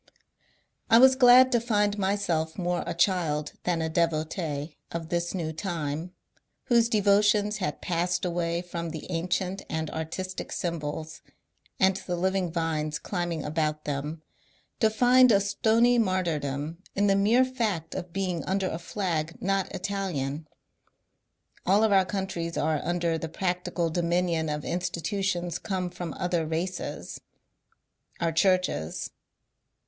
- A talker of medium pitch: Yes, medium, 175 Hz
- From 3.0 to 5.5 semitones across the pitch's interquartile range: Yes, average, 3.3 semitones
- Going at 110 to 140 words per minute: Yes, slow, 135 wpm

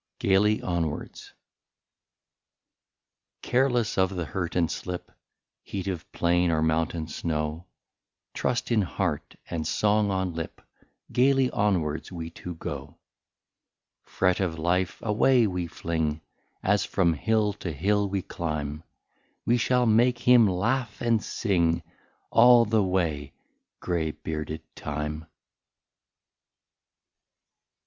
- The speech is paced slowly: Yes, slow, 115 wpm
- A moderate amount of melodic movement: Yes, average, 4.8 semitones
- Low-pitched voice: Yes, very low, 90 Hz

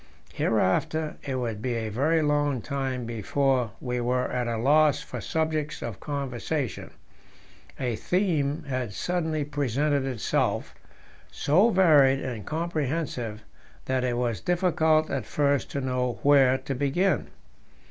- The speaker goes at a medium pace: No, slow, 130 wpm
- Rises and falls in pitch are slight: No, average, 3.8 semitones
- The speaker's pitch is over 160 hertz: No, medium, 140 Hz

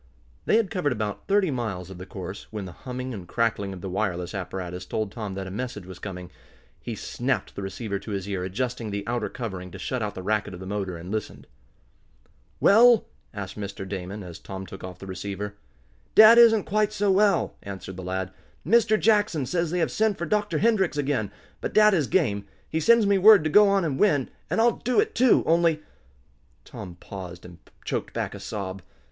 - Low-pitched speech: Yes, low, 110 Hz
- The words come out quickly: Yes, fast, 210 wpm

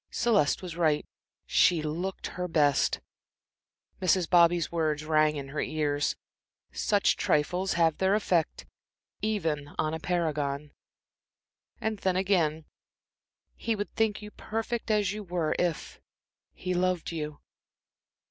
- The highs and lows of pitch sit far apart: No, average, 3.9 semitones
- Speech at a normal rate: No, slow, 125 wpm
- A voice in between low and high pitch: Yes, medium, 170 Hz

